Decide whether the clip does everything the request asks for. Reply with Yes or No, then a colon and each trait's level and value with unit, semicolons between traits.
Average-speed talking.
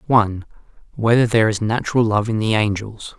Yes: average, 170 wpm